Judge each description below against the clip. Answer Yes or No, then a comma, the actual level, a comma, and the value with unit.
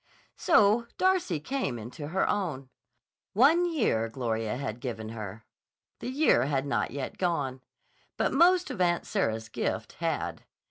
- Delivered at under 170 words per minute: Yes, average, 140 wpm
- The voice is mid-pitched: Yes, medium, 145 Hz